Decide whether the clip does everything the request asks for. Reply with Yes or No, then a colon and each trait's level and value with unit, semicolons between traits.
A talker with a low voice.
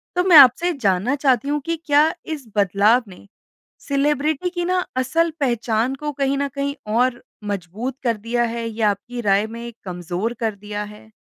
No: high, 245 Hz